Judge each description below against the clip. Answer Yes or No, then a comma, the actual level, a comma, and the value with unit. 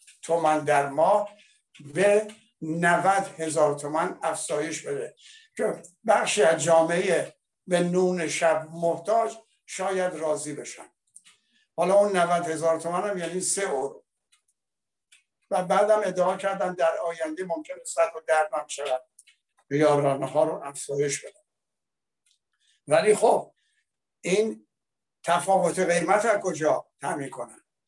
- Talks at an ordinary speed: Yes, average, 115 wpm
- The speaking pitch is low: No, medium, 175 Hz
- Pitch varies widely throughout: No, average, 4.2 semitones